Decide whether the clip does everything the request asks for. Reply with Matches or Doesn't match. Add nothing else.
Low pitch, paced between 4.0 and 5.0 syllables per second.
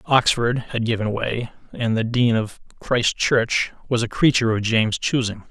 Matches